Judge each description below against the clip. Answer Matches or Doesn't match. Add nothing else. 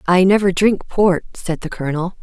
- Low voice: Doesn't match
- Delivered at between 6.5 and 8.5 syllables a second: Doesn't match